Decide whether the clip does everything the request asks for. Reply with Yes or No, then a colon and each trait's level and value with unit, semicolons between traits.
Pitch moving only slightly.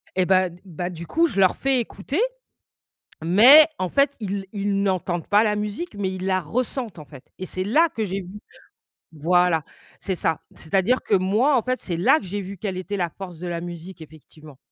No: average, 3.2 semitones